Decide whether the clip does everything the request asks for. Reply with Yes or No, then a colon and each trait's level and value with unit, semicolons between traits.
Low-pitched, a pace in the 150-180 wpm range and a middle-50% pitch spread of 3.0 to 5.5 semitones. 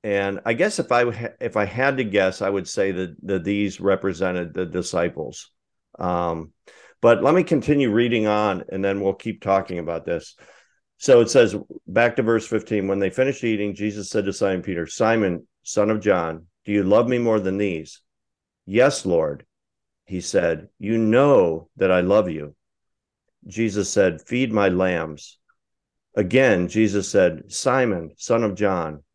Yes: low, 100 Hz; average, 170 wpm; average, 3.5 semitones